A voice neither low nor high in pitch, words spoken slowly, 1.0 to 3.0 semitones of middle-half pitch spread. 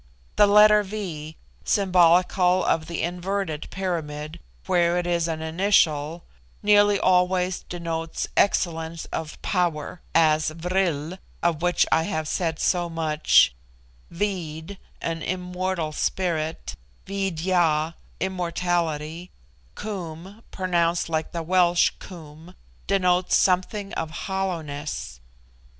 Yes: medium, 175 Hz; slow, 105 wpm; narrow, 2.6 semitones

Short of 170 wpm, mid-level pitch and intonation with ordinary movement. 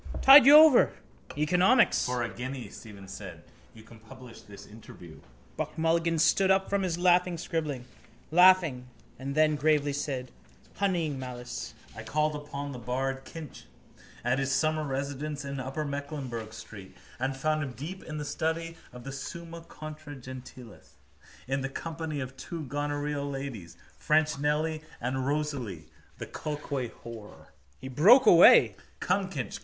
Yes: average, 150 wpm; medium, 145 Hz; average, 3.9 semitones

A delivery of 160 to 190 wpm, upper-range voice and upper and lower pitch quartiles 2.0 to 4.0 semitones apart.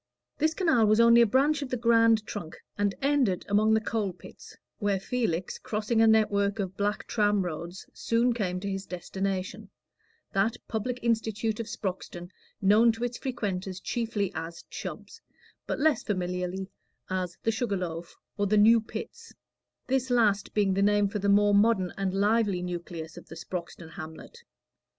Yes: average, 165 wpm; high, 205 Hz; average, 3.5 semitones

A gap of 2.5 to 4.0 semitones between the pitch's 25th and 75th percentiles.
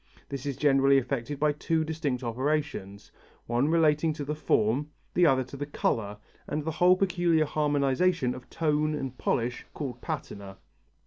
Yes: average, 3.3 semitones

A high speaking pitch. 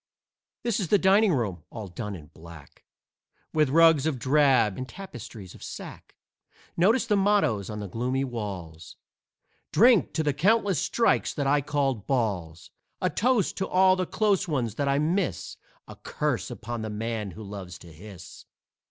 No: low, 130 Hz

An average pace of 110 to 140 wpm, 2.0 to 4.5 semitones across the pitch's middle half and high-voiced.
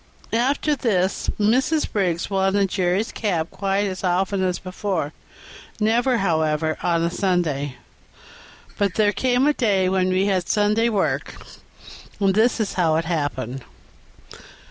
Yes: slow, 135 wpm; average, 3.2 semitones; high, 195 Hz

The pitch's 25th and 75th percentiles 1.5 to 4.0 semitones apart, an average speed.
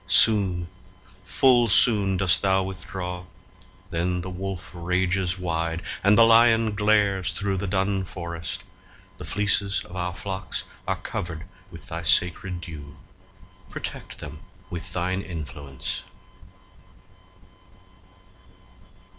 No: narrow, 2.4 semitones; slow, 110 wpm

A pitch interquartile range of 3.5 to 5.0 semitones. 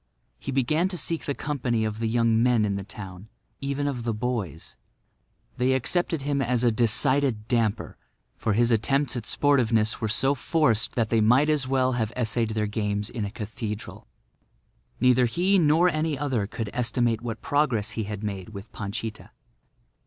Yes: average, 4.1 semitones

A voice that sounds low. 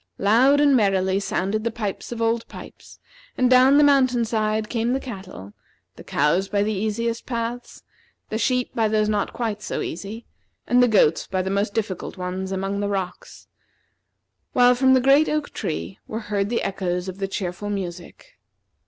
No: high, 215 Hz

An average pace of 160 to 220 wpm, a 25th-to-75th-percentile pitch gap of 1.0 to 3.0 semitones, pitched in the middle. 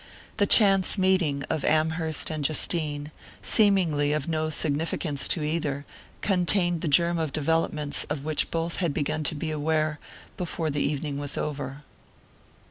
No: average, 145 wpm; narrow, 2.4 semitones; medium, 155 Hz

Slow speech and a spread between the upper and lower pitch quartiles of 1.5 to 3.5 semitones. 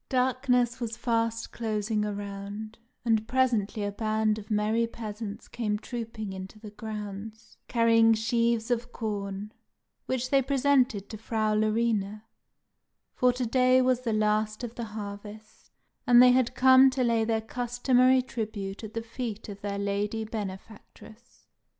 No: average, 145 wpm; narrow, 2.4 semitones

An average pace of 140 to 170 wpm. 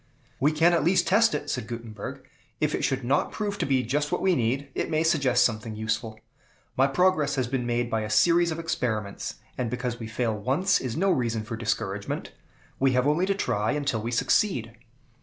No: fast, 205 wpm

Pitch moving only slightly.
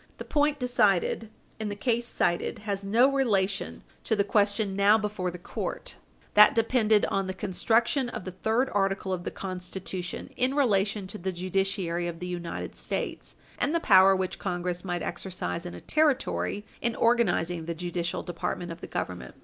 No: average, 3.7 semitones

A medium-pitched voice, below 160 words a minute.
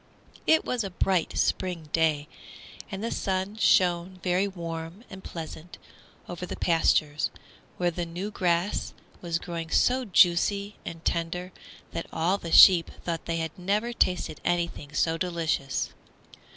Yes: medium, 175 Hz; average, 140 wpm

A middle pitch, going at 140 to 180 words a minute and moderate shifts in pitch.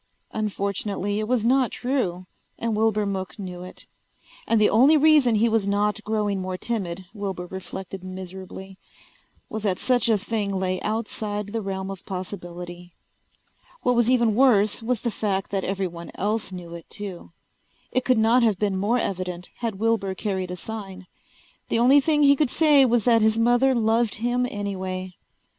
No: high, 210 Hz; average, 170 wpm; average, 3.5 semitones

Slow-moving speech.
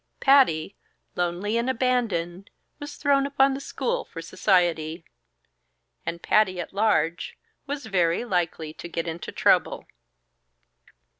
Yes: slow, 120 wpm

